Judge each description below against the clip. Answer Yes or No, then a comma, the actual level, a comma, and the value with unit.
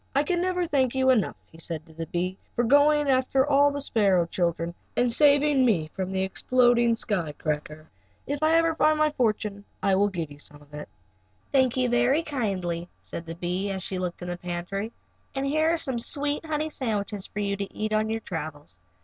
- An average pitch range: No, wide, 7.8 semitones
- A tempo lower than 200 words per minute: No, fast, 205 wpm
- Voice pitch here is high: Yes, high, 215 Hz